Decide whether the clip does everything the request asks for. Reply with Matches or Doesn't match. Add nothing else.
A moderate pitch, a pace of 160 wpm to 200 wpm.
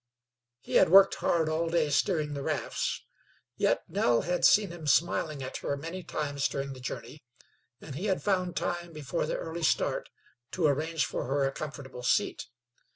Matches